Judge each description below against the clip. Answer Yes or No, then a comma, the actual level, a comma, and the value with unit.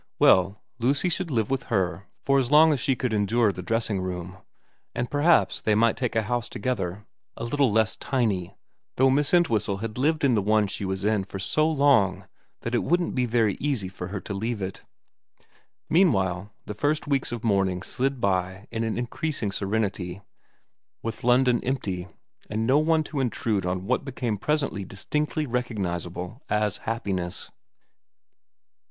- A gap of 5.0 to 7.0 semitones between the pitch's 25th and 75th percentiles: Yes, wide, 5.4 semitones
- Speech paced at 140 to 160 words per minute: No, average, 170 wpm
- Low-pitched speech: Yes, low, 115 Hz